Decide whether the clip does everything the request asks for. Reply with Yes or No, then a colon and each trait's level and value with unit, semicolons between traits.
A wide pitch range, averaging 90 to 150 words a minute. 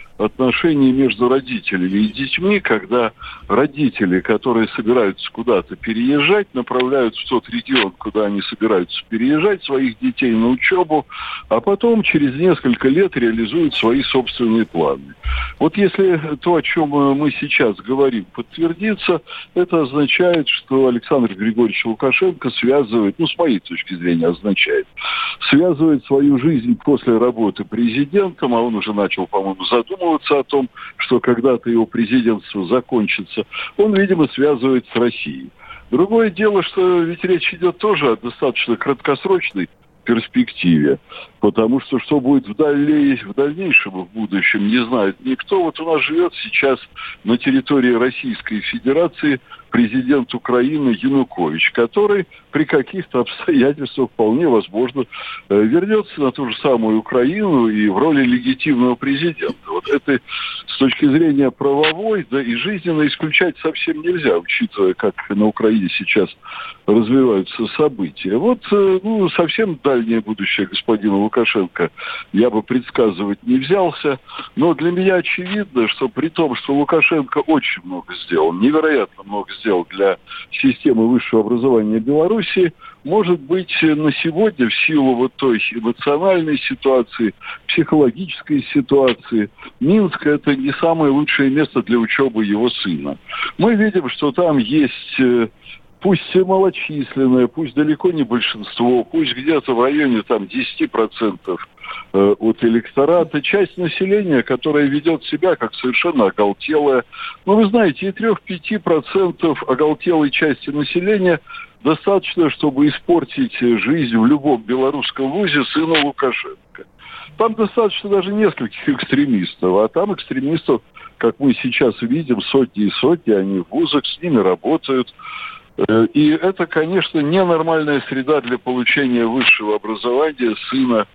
Yes: wide, 8.0 semitones; average, 130 wpm